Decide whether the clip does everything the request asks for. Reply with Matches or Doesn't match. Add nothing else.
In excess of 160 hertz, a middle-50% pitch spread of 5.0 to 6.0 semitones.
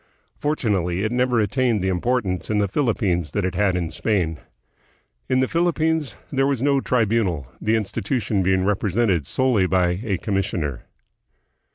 Doesn't match